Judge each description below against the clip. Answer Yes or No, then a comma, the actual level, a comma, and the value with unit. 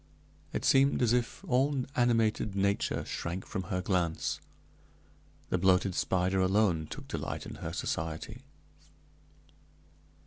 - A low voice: Yes, very low, 95 Hz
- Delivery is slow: Yes, slow, 115 wpm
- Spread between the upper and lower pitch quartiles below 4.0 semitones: No, average, 4.5 semitones